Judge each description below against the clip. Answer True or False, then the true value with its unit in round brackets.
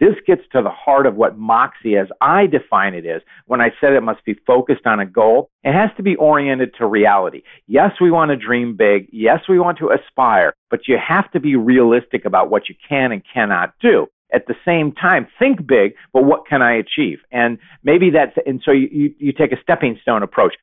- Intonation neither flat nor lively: False (6.0 semitones)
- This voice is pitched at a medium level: True (150 Hz)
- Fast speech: True (225 wpm)